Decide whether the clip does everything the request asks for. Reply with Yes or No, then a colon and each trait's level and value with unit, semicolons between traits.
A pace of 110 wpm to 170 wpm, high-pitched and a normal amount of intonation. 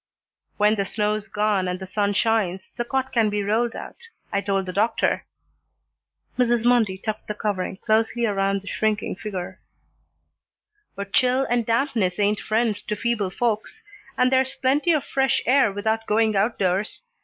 Yes: average, 160 wpm; high, 215 Hz; average, 3.1 semitones